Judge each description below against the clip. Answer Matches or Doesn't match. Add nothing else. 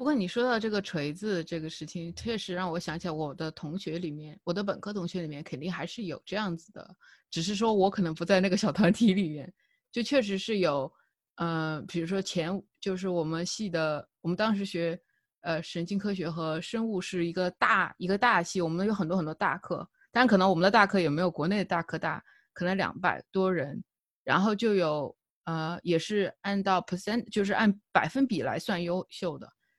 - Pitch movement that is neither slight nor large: Matches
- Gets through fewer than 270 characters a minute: Doesn't match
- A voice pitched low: Doesn't match